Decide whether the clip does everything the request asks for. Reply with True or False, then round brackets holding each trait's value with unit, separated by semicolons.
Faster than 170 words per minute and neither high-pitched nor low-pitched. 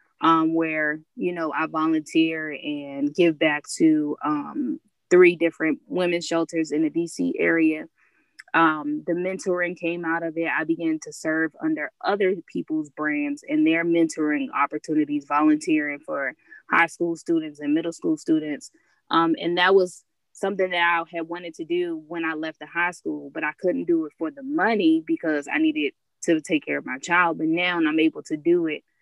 True (180 wpm; 170 Hz)